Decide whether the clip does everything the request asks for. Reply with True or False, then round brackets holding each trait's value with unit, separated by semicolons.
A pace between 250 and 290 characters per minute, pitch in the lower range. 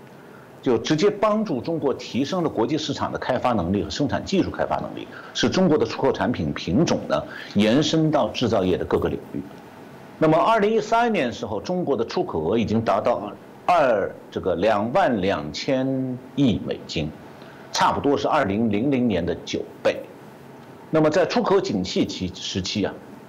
False (265 characters per minute; 155 Hz)